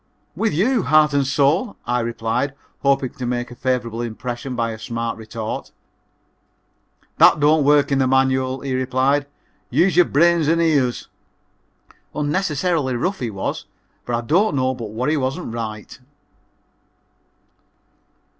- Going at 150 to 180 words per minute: No, average, 140 wpm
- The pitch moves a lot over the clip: No, average, 3.8 semitones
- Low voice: Yes, low, 130 Hz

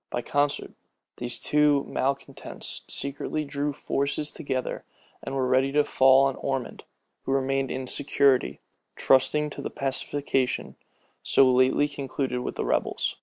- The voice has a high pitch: No, low, 135 Hz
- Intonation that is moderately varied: No, narrow, 1.6 semitones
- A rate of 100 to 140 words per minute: Yes, slow, 135 wpm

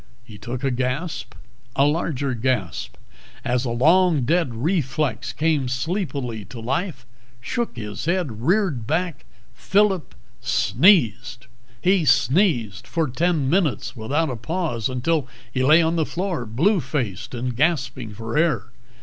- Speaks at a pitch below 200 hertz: Yes, low, 135 Hz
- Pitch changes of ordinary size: No, wide, 5.7 semitones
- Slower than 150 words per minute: Yes, slow, 135 wpm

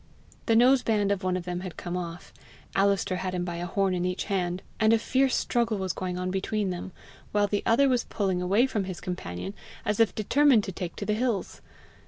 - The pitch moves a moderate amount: Yes, average, 3.4 semitones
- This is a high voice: Yes, high, 195 Hz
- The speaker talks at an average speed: No, fast, 225 wpm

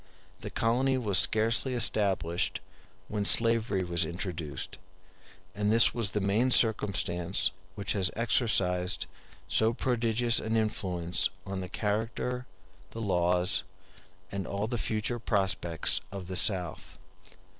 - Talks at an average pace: No, slow, 125 wpm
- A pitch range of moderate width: Yes, average, 3.9 semitones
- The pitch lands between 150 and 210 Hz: No, low, 105 Hz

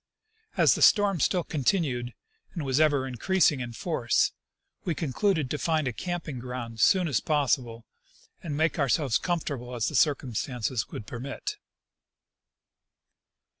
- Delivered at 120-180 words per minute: Yes, average, 140 wpm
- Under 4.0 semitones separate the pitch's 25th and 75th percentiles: No, average, 5.0 semitones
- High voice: No, medium, 140 Hz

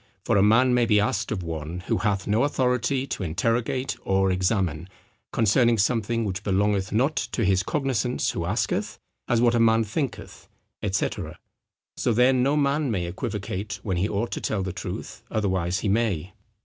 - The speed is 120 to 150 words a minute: No, average, 175 wpm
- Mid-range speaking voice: No, low, 105 Hz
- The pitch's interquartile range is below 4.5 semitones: Yes, average, 4.1 semitones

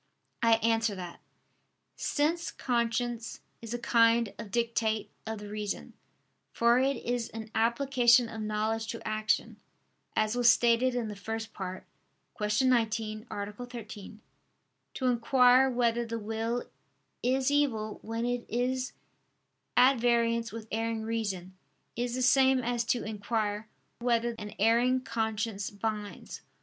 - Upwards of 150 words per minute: No, slow, 135 wpm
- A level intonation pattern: Yes, narrow, 2.1 semitones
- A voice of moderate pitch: No, high, 230 Hz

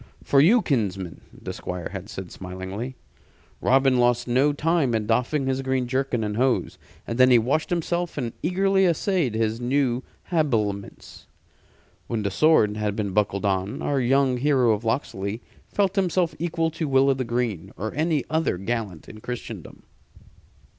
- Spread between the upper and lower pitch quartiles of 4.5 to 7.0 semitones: Yes, wide, 5.6 semitones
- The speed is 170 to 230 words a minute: No, average, 160 wpm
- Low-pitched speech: Yes, low, 125 Hz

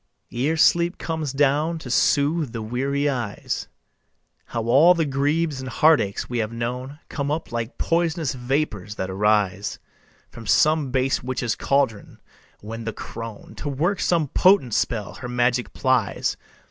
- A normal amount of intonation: Yes, average, 4.8 semitones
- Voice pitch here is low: Yes, low, 130 Hz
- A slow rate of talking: No, average, 145 wpm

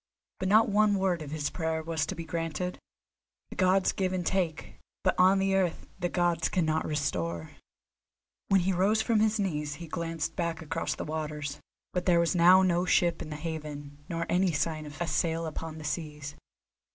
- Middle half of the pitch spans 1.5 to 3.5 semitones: Yes, average, 3.2 semitones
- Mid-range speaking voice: Yes, medium, 165 Hz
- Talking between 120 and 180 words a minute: No, average, 190 wpm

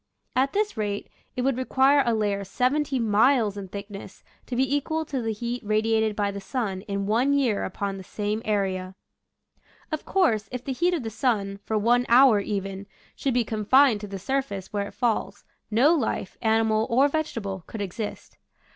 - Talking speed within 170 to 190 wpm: Yes, average, 185 wpm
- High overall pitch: Yes, high, 225 Hz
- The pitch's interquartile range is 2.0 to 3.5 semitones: No, average, 4.5 semitones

